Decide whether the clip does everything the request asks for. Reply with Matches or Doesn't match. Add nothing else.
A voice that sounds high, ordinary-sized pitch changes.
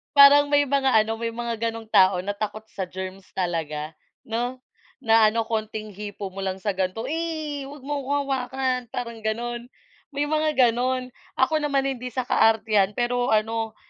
Matches